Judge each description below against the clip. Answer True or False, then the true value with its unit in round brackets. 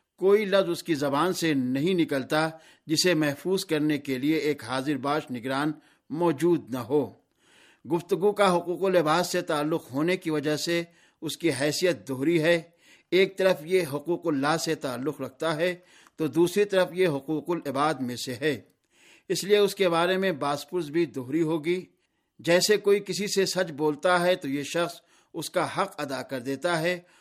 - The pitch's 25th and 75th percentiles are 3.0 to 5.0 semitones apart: True (3.3 semitones)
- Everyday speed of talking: True (175 wpm)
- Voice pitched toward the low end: False (165 Hz)